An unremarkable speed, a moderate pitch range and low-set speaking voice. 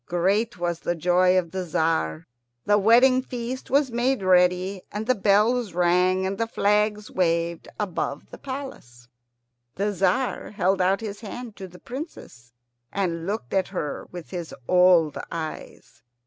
No: average, 150 wpm; average, 3.8 semitones; high, 190 Hz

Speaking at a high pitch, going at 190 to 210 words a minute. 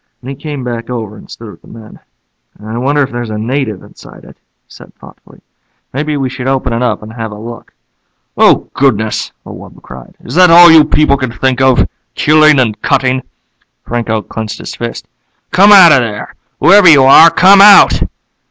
No: low, 130 Hz; average, 195 wpm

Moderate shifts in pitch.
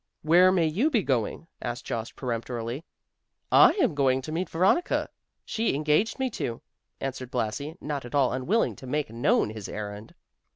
No: wide, 6.4 semitones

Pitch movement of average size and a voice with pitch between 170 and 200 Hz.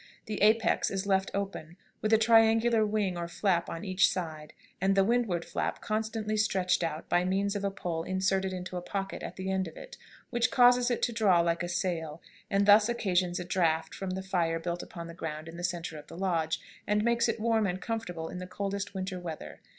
Yes: average, 3.5 semitones; high, 190 Hz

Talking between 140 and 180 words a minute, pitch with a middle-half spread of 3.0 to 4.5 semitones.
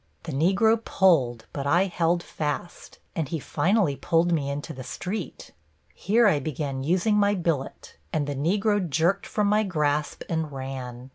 No: average, 160 wpm; average, 5.3 semitones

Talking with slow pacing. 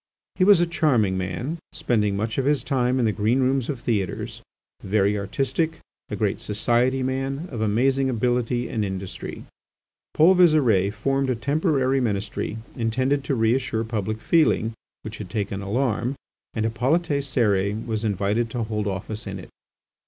No: average, 155 wpm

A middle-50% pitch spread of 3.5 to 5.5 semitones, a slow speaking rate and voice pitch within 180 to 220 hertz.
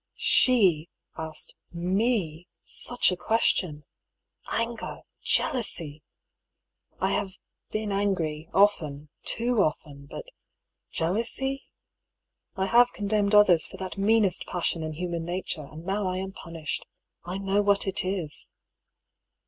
Yes: average, 4.1 semitones; slow, 120 wpm; high, 190 Hz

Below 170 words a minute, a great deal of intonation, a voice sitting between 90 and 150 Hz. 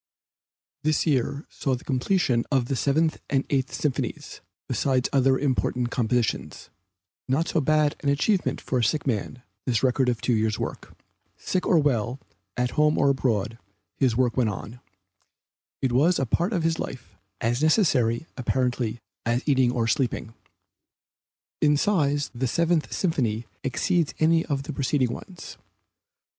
No: average, 150 wpm; average, 3.8 semitones; low, 135 Hz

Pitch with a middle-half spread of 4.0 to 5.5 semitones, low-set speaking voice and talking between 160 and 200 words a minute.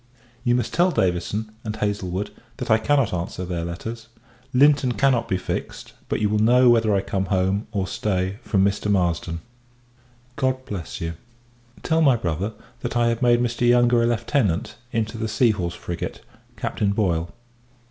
Yes: average, 4.5 semitones; low, 110 Hz; average, 170 wpm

